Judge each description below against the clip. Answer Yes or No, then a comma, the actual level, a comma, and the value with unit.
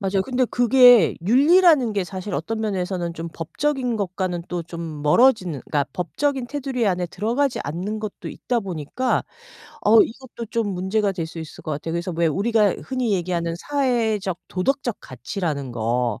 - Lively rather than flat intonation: Yes, wide, 6.1 semitones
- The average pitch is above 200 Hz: No, high, 195 Hz